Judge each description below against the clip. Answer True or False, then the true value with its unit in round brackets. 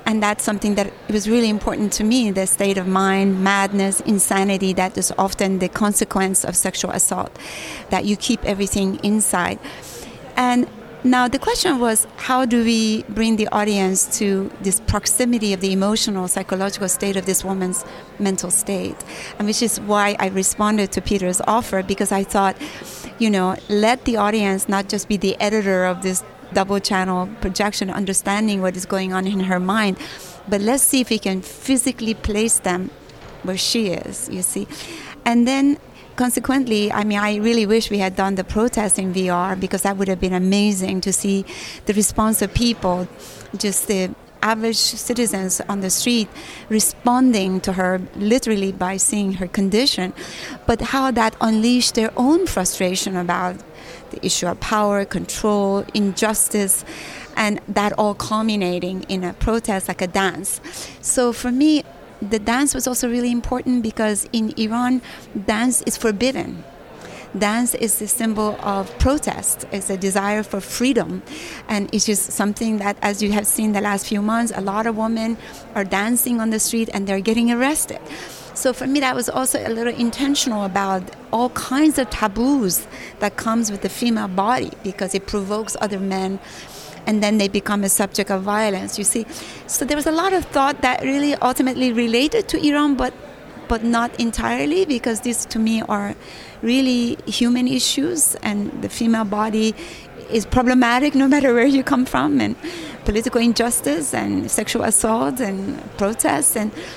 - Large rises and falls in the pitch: False (3.4 semitones)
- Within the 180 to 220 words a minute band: False (170 wpm)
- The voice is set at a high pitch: True (215 Hz)